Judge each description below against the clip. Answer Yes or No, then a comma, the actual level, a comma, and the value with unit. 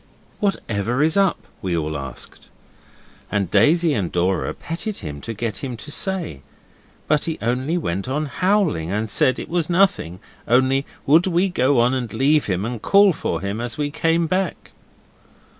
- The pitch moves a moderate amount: No, wide, 8.5 semitones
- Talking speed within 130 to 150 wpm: No, average, 170 wpm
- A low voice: Yes, low, 130 Hz